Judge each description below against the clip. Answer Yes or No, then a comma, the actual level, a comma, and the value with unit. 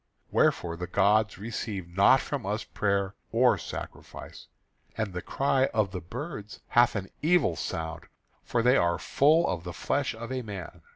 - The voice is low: Yes, low, 105 Hz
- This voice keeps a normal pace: Yes, average, 165 wpm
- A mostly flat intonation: No, average, 5.1 semitones